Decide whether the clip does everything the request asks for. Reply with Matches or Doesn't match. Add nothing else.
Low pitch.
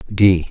Matches